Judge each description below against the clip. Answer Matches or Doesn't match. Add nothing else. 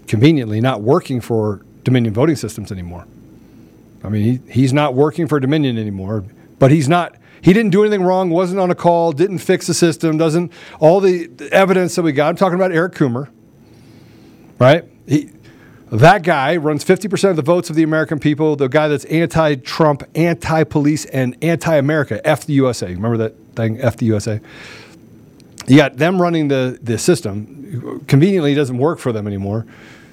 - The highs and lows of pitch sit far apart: Matches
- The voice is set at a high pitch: Doesn't match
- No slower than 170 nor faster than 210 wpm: Matches